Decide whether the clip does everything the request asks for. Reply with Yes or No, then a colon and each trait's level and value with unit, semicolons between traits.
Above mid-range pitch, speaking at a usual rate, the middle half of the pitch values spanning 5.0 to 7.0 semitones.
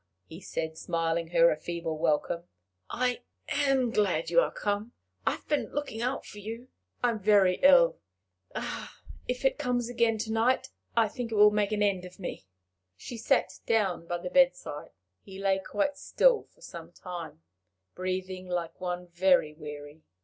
Yes: high, 200 Hz; average, 170 wpm; wide, 5.6 semitones